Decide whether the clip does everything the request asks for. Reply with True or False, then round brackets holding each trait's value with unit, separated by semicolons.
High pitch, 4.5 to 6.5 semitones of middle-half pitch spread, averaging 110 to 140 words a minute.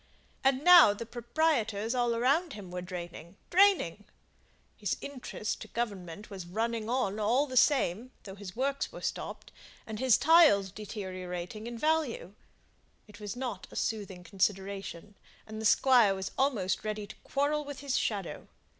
False (220 Hz; 5.1 semitones; 155 wpm)